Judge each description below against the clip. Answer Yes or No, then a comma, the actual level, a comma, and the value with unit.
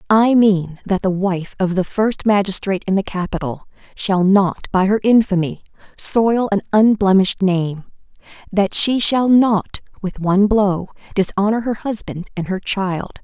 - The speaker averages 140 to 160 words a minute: Yes, average, 155 wpm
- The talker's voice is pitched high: Yes, high, 195 Hz